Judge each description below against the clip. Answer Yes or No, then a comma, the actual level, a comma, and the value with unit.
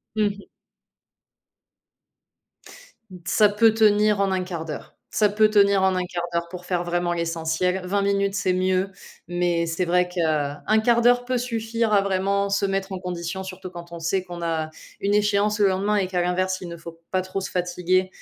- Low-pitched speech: No, medium, 185 Hz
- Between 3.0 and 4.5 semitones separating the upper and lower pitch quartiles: No, narrow, 2.5 semitones